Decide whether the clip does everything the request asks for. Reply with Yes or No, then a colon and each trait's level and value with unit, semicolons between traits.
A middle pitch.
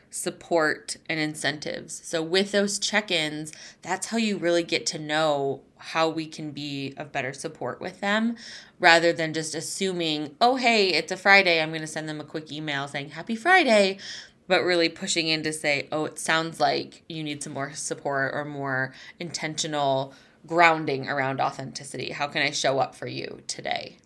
Yes: medium, 160 Hz